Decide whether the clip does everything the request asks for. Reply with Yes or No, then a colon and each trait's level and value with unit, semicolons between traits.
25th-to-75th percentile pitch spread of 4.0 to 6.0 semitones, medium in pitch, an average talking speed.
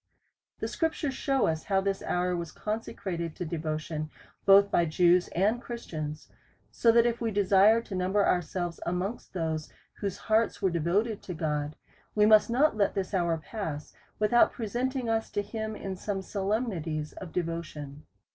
No: average, 4.6 semitones; high, 195 Hz; average, 165 wpm